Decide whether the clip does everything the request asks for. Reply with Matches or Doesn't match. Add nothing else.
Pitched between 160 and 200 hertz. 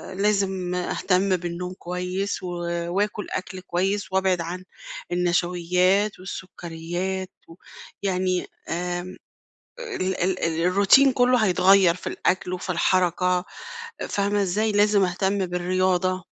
Matches